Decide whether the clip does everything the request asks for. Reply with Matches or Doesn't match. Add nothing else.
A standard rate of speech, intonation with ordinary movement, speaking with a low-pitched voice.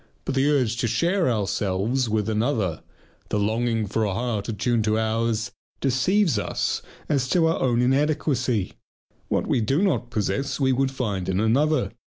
Matches